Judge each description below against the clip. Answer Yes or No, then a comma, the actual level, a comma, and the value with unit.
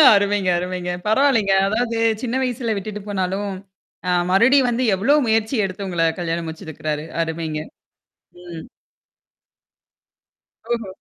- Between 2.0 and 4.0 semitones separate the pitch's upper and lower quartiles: No, average, 4.5 semitones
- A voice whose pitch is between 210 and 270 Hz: No, high, 195 Hz